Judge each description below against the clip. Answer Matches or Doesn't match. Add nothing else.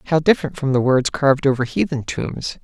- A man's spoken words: Matches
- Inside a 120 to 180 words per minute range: Doesn't match